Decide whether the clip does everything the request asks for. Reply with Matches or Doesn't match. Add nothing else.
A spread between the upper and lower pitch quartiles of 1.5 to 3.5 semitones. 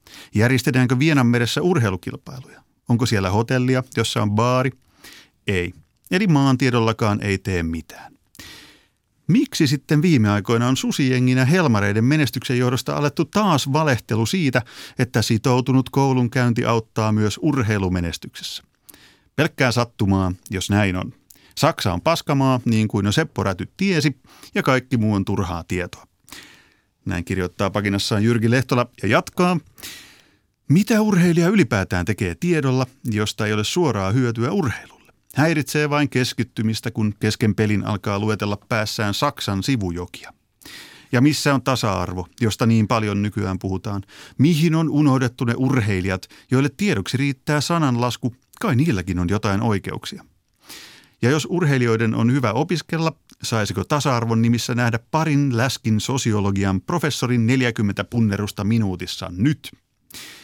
Doesn't match